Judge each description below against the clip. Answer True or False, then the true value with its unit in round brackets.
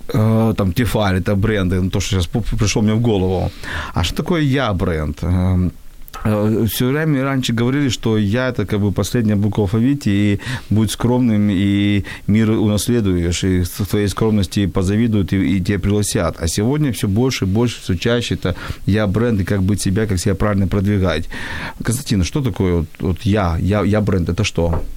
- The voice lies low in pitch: True (105 Hz)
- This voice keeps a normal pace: False (175 wpm)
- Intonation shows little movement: False (3.2 semitones)